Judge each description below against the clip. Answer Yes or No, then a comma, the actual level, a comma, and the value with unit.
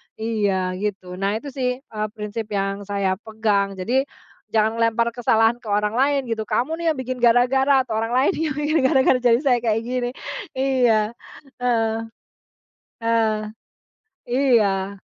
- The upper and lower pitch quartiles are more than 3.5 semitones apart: No, average, 3.2 semitones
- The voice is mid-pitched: No, high, 230 Hz